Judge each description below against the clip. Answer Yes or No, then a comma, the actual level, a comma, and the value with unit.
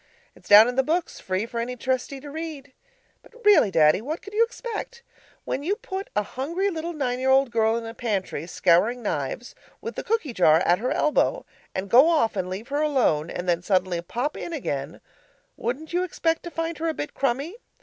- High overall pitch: Yes, very high, 260 Hz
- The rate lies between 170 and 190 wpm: No, fast, 205 wpm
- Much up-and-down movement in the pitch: Yes, wide, 7.9 semitones